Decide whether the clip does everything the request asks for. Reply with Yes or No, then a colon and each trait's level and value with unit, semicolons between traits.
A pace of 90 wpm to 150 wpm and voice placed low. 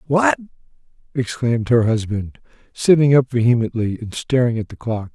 Yes: average, 140 wpm; low, 125 Hz